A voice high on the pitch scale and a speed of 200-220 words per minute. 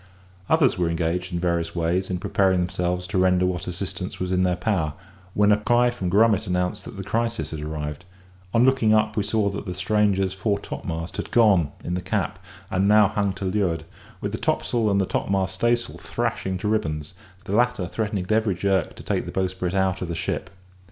No: very low, 95 Hz; fast, 205 wpm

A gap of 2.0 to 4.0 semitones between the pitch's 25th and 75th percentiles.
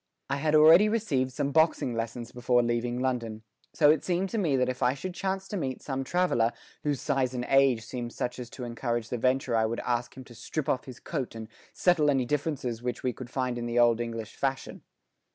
Yes: average, 3.7 semitones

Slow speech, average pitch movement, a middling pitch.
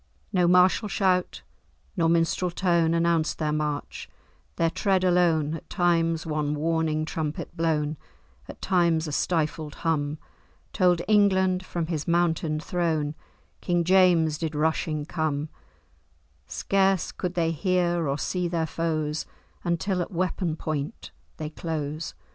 No: slow, 130 wpm; narrow, 2.3 semitones; medium, 165 Hz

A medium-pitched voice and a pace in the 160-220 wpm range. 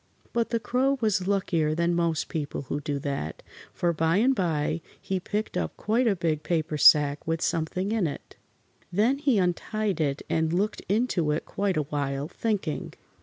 Yes: medium, 170 Hz; average, 175 wpm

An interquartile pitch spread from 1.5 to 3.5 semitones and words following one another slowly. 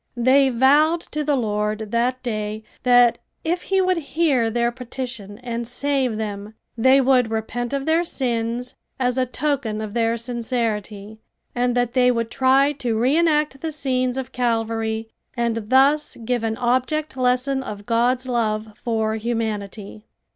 No: average, 2.9 semitones; average, 155 wpm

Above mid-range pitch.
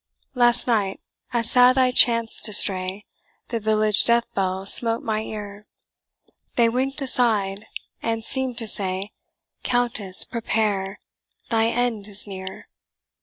Yes: high, 220 Hz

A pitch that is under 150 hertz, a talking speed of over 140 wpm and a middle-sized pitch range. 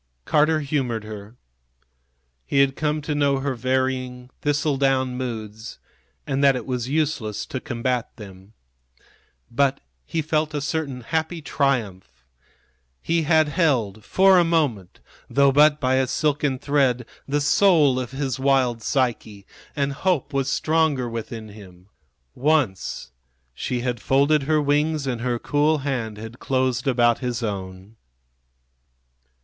No: low, 135 Hz; slow, 135 wpm; average, 3.8 semitones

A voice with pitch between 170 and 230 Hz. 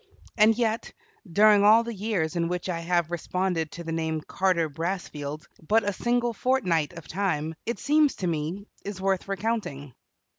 Yes: medium, 185 Hz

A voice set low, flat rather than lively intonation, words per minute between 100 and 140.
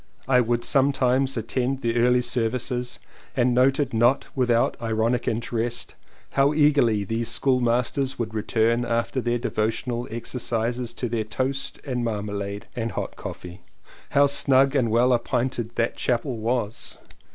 Yes: low, 120 Hz; narrow, 2.1 semitones; slow, 135 wpm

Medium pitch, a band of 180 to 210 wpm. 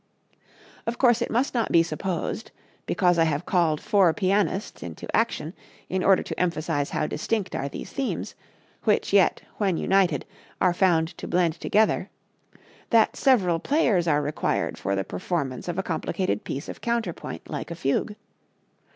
No: medium, 180 Hz; average, 160 wpm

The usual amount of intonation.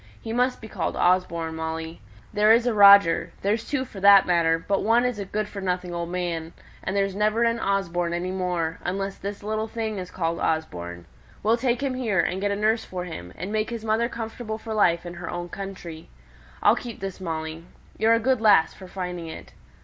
Yes: average, 4.2 semitones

